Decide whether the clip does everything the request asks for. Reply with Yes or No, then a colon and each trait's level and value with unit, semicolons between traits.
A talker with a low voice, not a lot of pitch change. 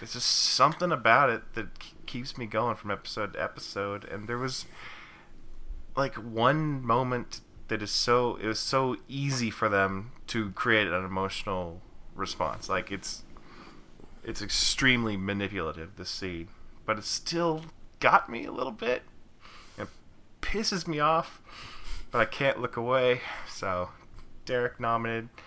No: low, 115 Hz; average, 4.2 semitones